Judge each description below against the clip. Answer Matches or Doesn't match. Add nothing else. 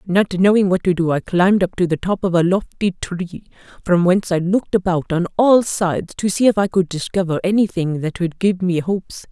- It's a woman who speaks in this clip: Matches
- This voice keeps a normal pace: Doesn't match